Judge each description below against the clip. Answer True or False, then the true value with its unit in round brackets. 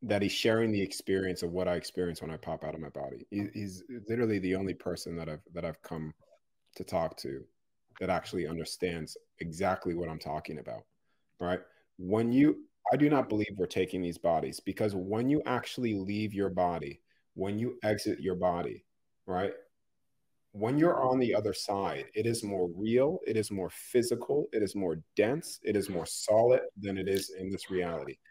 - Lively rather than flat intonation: False (4.1 semitones)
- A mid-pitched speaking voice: False (100 Hz)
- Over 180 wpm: True (190 wpm)